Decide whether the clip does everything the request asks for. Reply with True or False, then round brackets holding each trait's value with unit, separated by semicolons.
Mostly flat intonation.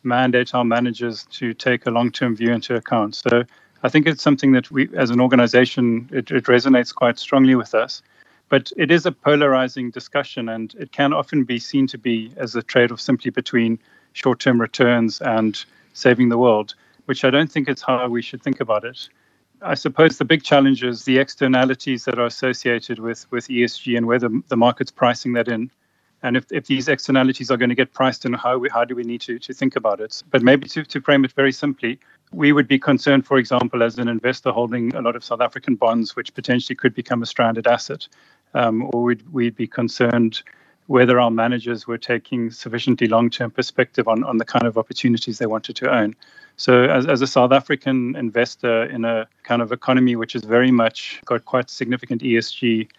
True (1.9 semitones)